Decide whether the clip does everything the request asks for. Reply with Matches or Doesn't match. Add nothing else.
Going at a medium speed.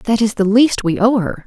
Doesn't match